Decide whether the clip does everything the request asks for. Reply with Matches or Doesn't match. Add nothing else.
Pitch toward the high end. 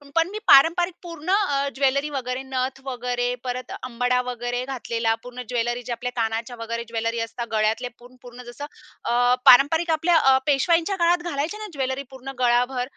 Matches